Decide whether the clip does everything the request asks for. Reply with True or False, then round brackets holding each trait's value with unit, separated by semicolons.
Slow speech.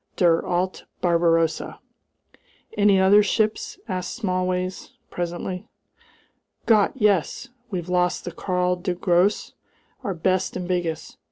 True (110 wpm)